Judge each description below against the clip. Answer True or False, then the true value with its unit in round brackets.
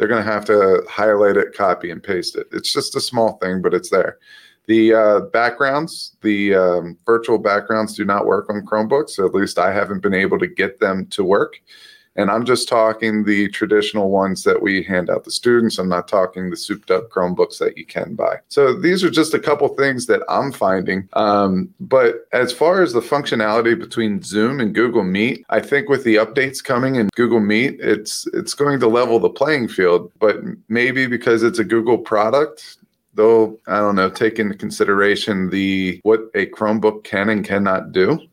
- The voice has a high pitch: False (115 Hz)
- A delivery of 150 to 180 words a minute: False (200 wpm)